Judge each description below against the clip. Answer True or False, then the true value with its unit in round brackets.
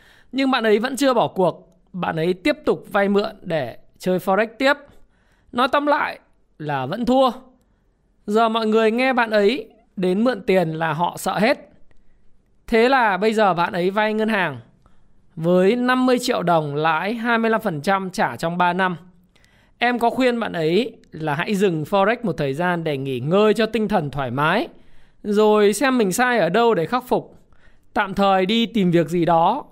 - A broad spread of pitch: False (4.9 semitones)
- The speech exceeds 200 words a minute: False (185 wpm)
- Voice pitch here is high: True (210 Hz)